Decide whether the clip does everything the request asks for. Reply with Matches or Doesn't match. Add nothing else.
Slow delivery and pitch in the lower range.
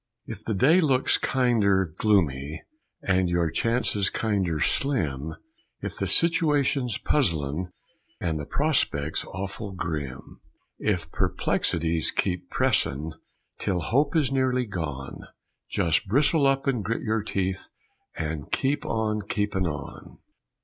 Matches